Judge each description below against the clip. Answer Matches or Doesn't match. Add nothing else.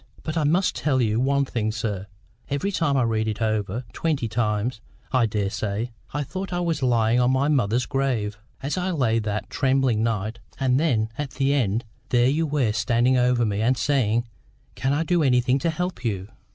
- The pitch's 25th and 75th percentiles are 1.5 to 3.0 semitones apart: Doesn't match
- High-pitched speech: Doesn't match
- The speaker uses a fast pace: Doesn't match